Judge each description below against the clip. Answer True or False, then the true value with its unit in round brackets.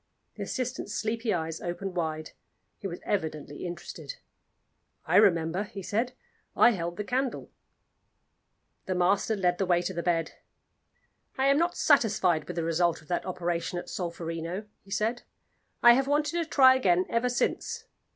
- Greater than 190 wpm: False (160 wpm)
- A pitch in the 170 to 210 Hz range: True (190 Hz)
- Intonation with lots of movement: True (5.7 semitones)